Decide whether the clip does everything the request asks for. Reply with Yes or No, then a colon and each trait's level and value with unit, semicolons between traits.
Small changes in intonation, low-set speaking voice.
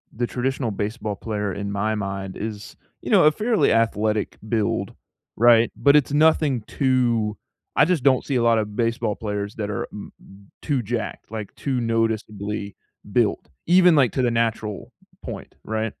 No: average, 3.4 semitones; low, 115 Hz